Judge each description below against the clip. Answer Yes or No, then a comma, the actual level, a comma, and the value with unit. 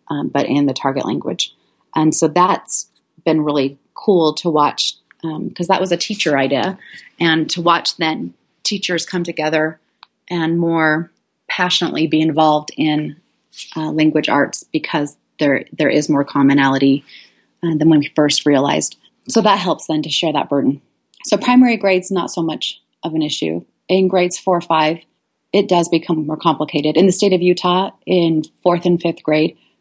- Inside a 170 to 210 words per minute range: Yes, average, 175 wpm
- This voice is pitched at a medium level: Yes, medium, 160 Hz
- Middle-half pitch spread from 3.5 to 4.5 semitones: No, average, 2.7 semitones